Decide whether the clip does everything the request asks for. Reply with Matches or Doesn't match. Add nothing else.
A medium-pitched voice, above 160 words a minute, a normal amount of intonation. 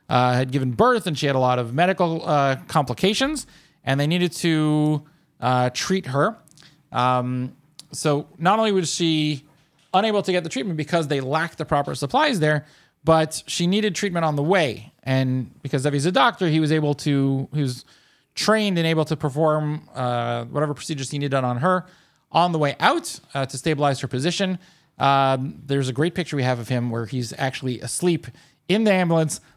Matches